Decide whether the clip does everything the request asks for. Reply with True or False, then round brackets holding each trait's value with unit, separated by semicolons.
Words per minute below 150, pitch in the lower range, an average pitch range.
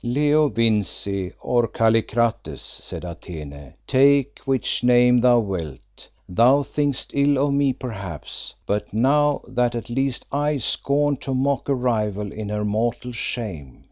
True (140 wpm; 120 Hz; 4.7 semitones)